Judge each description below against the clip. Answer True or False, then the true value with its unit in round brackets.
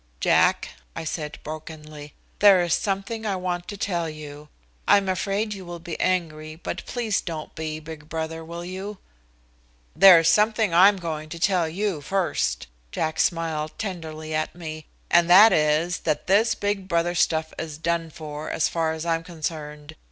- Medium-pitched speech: True (165 Hz)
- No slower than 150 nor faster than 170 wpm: True (165 wpm)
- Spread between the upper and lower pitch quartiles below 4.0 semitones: True (3.2 semitones)